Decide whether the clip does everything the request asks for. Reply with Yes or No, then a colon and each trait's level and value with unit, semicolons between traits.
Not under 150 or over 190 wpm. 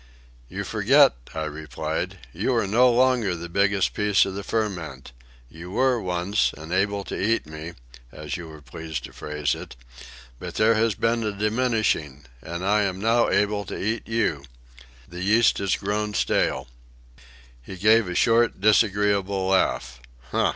Yes: average, 160 wpm